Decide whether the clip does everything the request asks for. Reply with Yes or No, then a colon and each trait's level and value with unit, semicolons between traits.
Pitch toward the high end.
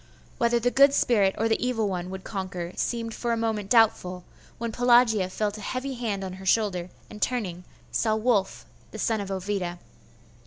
Yes: high, 215 Hz